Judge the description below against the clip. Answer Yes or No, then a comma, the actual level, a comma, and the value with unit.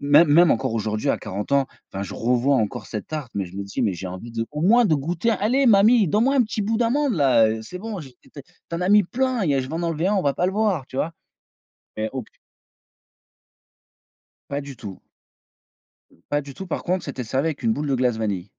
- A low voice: No, medium, 145 Hz